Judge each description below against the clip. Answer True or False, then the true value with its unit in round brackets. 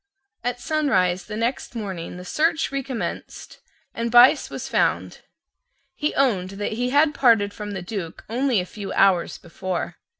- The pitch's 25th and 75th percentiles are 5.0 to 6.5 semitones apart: True (5.3 semitones)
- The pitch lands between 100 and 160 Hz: False (220 Hz)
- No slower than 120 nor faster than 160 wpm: True (155 wpm)